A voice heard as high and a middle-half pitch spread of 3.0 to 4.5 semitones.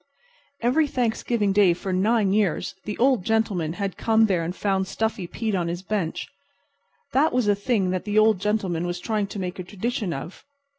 Yes: high, 205 Hz; average, 3.3 semitones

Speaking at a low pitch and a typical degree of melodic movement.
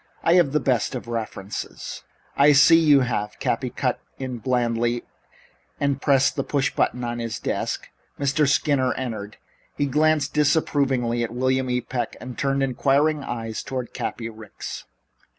Yes: low, 130 Hz; average, 3.1 semitones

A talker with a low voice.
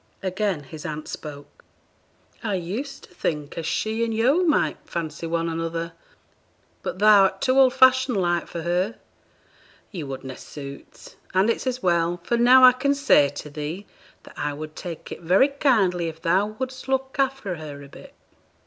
No: medium, 185 Hz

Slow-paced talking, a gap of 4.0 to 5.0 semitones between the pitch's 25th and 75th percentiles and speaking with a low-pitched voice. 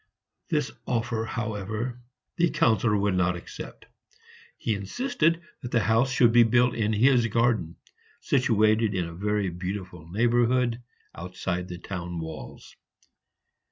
Yes: slow, 125 wpm; average, 4.5 semitones; low, 110 Hz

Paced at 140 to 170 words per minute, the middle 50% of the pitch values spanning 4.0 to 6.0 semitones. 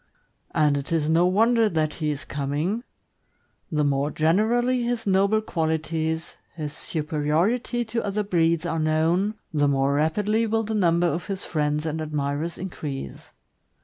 Yes: average, 145 wpm; average, 5.3 semitones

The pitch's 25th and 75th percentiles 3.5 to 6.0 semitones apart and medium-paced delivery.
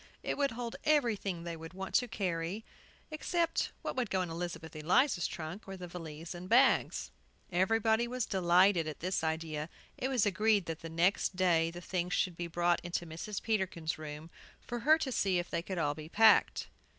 Yes: average, 4.9 semitones; average, 190 wpm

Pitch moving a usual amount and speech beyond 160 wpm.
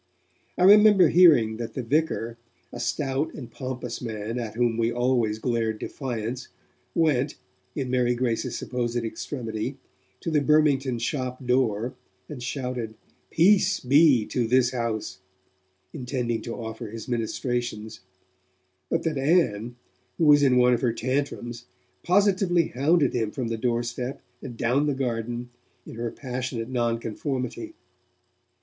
No: average, 3.3 semitones; slow, 135 wpm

